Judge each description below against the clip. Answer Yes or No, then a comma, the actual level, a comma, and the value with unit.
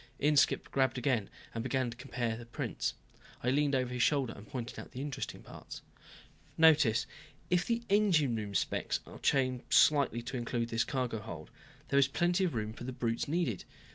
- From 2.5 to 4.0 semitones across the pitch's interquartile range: Yes, average, 3.6 semitones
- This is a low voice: Yes, low, 130 Hz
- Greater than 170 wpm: Yes, average, 185 wpm